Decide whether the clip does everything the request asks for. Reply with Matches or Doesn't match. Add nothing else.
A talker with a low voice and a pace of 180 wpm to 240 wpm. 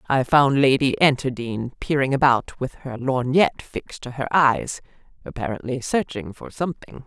Doesn't match